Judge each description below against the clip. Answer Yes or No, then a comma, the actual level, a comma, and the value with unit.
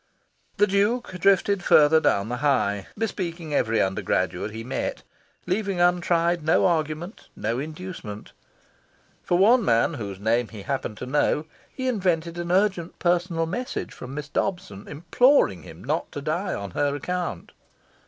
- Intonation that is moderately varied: No, wide, 7.0 semitones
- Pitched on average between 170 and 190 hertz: No, medium, 160 Hz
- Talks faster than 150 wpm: No, average, 145 wpm